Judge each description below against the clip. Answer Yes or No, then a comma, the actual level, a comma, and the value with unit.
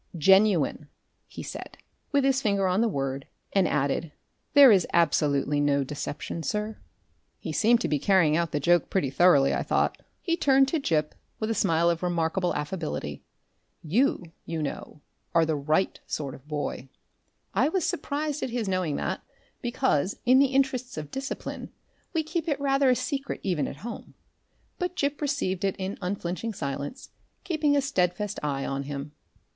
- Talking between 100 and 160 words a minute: No, average, 170 wpm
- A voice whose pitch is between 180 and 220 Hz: Yes, medium, 185 Hz